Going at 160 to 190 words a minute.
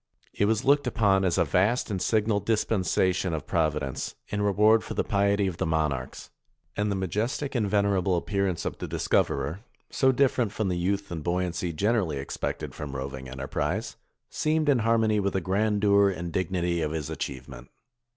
Yes: average, 180 wpm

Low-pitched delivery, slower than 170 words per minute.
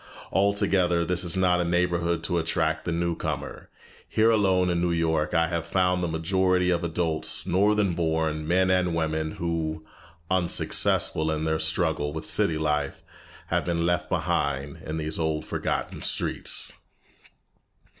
Yes: very low, 85 Hz; average, 155 wpm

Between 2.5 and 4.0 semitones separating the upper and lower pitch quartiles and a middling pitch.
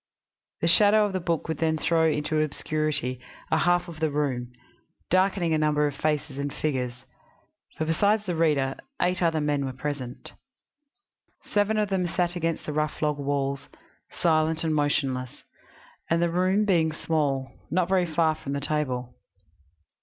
Yes: average, 3.1 semitones; medium, 155 Hz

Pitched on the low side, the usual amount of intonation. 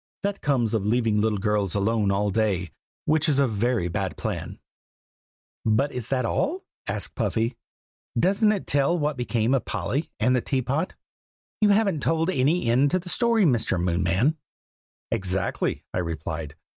No: low, 120 Hz; wide, 6.8 semitones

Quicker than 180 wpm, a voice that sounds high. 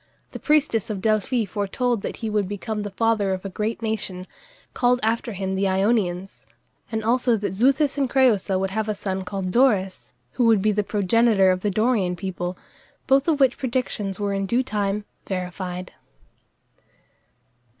No: average, 170 wpm; high, 210 Hz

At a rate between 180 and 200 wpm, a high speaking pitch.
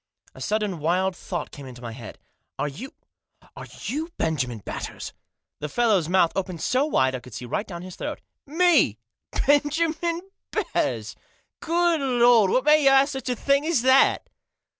Yes: average, 185 wpm; high, 230 Hz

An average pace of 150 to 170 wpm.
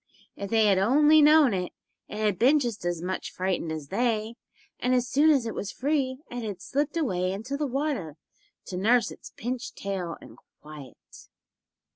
No: average, 180 wpm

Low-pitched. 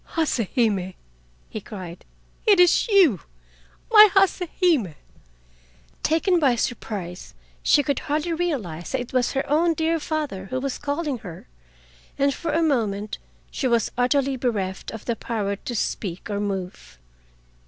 No: very high, 255 Hz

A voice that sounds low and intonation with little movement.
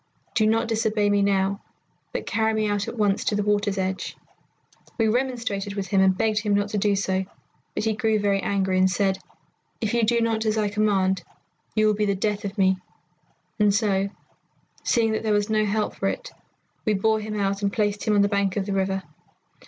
No: high, 205 Hz; narrow, 1.7 semitones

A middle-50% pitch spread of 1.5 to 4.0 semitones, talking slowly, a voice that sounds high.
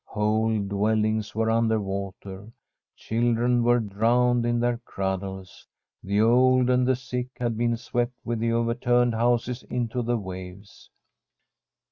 No: narrow, 2.5 semitones; slow, 130 wpm; low, 115 Hz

